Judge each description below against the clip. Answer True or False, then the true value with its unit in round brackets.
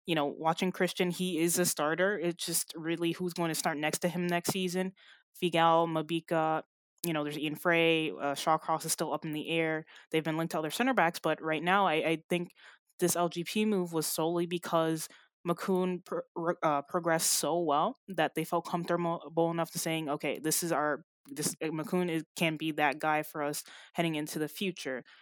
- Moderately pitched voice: True (165 Hz)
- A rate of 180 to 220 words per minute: True (200 wpm)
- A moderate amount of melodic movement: False (2.1 semitones)